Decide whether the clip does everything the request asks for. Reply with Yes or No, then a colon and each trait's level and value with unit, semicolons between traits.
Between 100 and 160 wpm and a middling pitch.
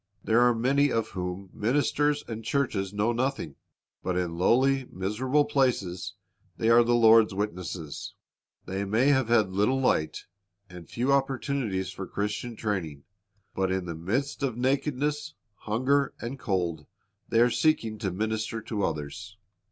No: average, 145 wpm; low, 110 Hz